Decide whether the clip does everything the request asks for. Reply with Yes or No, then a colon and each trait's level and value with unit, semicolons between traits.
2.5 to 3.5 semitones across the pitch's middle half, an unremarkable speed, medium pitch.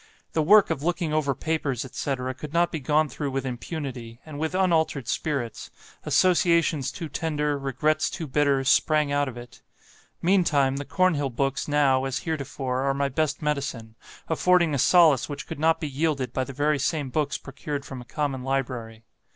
Yes: average, 2.9 semitones; average, 175 wpm; medium, 145 Hz